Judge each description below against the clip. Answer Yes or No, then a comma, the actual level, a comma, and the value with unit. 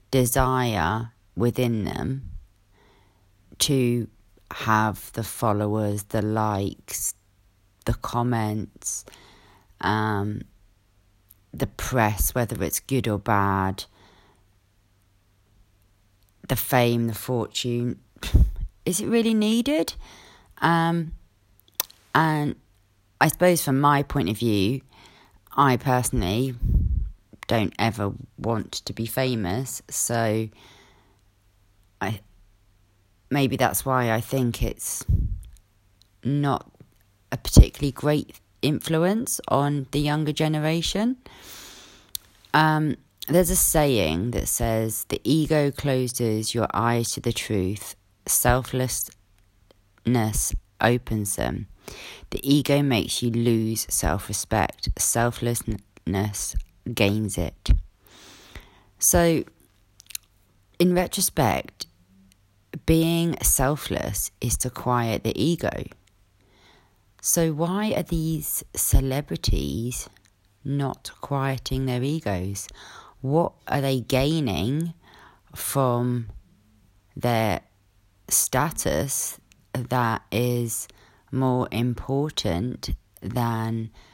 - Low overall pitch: Yes, low, 110 Hz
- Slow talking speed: Yes, slow, 85 wpm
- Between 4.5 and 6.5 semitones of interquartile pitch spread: Yes, average, 4.9 semitones